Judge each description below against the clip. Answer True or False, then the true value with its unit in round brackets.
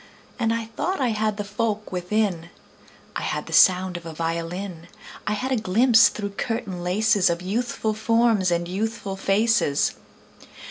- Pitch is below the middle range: False (205 Hz)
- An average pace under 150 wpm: False (155 wpm)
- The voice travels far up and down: False (3.9 semitones)